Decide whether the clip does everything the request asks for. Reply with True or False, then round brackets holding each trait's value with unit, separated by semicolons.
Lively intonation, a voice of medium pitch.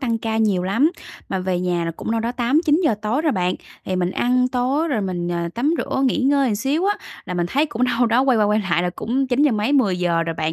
False (6.6 semitones; 230 Hz)